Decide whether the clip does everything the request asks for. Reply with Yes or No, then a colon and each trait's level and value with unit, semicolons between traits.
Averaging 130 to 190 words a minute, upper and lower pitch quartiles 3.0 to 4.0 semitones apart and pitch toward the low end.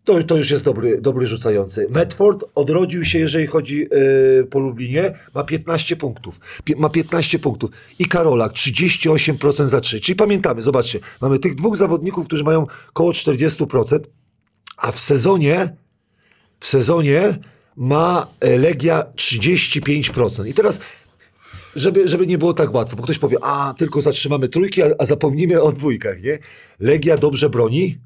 No: average, 150 wpm; average, 3.7 semitones; medium, 150 Hz